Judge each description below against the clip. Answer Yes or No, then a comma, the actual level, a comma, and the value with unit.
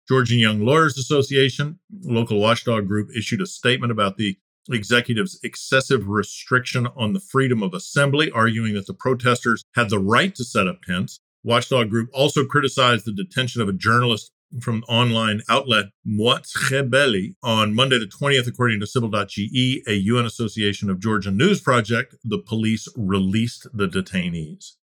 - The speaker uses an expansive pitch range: No, average, 3.4 semitones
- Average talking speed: Yes, average, 155 wpm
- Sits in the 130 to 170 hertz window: No, low, 120 Hz